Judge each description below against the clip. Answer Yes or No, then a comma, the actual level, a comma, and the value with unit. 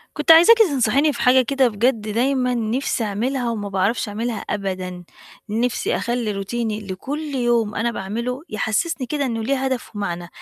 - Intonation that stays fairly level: No, average, 4.0 semitones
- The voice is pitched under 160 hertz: No, high, 235 Hz